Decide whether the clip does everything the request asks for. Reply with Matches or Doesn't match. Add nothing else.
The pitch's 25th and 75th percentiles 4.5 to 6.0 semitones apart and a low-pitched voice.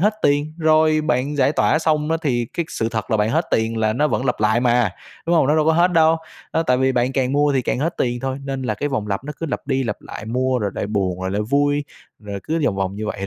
Matches